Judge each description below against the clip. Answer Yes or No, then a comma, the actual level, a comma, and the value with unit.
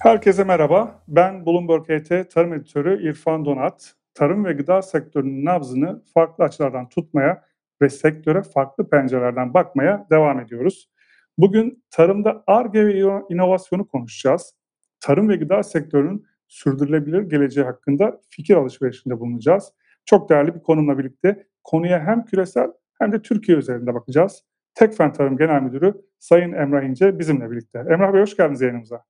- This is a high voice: No, medium, 165 Hz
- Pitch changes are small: No, average, 5.2 semitones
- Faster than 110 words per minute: Yes, fast, 140 wpm